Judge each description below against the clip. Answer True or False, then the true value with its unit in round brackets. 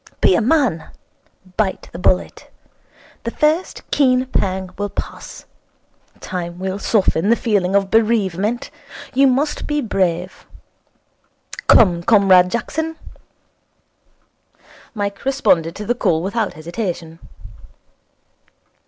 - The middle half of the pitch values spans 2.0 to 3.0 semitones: False (4.9 semitones)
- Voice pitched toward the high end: True (200 Hz)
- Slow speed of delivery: True (105 wpm)